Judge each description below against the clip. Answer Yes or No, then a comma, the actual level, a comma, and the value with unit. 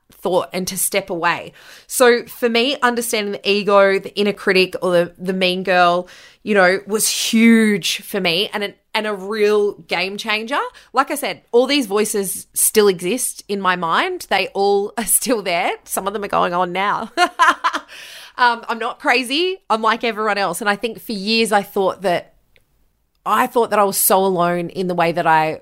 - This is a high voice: Yes, high, 205 Hz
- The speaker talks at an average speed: Yes, average, 195 wpm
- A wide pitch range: No, average, 3.6 semitones